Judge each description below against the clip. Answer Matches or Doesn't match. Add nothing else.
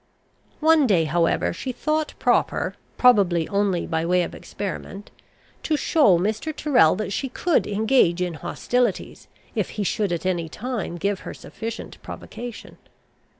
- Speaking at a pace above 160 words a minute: Doesn't match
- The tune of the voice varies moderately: Doesn't match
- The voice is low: Doesn't match